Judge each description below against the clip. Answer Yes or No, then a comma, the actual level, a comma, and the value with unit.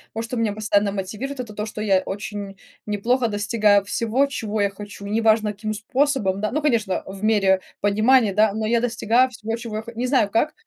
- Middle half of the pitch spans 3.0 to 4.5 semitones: No, narrow, 2.4 semitones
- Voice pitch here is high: Yes, high, 215 Hz